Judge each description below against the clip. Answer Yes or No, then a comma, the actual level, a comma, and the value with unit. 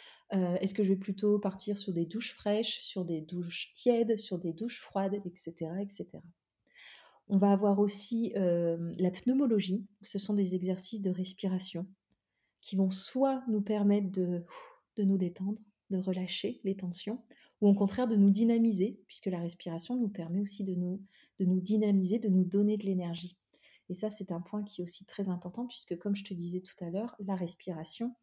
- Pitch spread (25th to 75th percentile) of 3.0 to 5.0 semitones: No, narrow, 2.5 semitones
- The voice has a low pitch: No, high, 195 Hz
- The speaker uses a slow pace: No, average, 190 wpm